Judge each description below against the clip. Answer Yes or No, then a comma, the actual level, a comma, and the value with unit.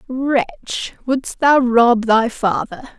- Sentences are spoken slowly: Yes, slow, 120 wpm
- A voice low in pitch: No, high, 240 Hz